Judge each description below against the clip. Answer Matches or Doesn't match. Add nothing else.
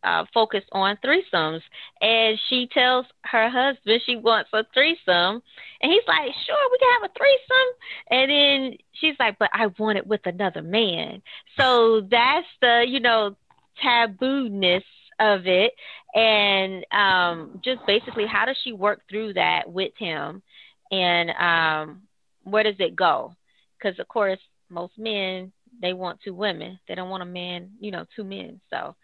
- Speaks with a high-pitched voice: Matches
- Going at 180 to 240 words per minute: Doesn't match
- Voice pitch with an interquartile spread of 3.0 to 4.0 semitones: Doesn't match